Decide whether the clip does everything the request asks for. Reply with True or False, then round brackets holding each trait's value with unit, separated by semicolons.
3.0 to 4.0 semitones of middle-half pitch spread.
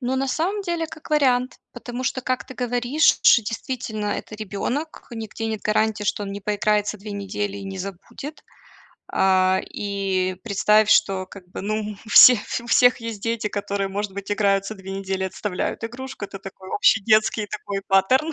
True (3.7 semitones)